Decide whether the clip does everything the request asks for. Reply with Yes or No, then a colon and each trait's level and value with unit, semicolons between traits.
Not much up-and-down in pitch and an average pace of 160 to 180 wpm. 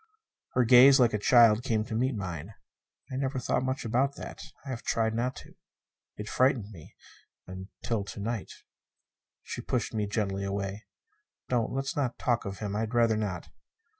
No: average, 3.6 semitones; average, 175 wpm